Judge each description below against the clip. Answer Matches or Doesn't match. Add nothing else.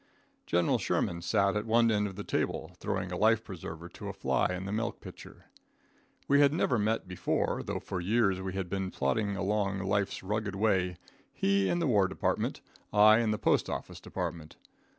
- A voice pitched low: Matches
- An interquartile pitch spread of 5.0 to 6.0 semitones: Doesn't match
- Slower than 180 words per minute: Doesn't match